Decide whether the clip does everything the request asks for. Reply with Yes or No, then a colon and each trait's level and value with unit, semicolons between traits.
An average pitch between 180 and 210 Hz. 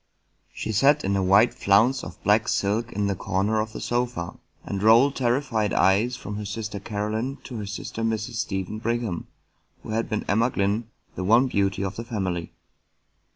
No: low, 110 Hz